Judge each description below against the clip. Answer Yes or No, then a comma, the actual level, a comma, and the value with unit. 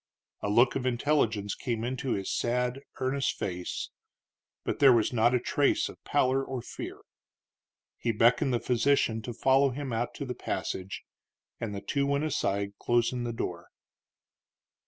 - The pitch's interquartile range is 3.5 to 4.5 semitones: No, average, 3.0 semitones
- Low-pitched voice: Yes, low, 120 Hz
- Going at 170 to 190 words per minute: No, average, 155 wpm